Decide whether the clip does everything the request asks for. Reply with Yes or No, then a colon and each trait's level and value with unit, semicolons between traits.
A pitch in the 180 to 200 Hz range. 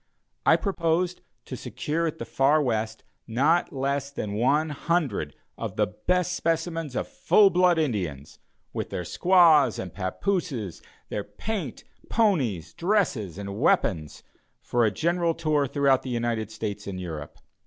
No: medium, 140 Hz